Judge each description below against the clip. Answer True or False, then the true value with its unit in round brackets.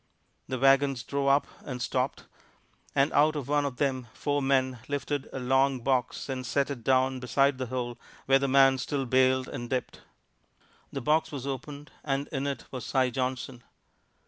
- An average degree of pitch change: False (1.6 semitones)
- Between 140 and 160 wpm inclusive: False (175 wpm)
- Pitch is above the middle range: False (135 Hz)